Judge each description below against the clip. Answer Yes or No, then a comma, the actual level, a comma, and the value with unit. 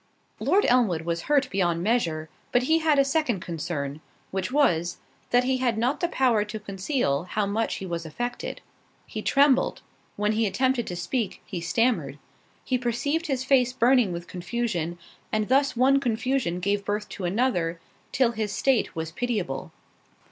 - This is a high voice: Yes, high, 220 Hz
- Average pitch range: No, wide, 6.6 semitones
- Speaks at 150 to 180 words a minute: Yes, average, 160 wpm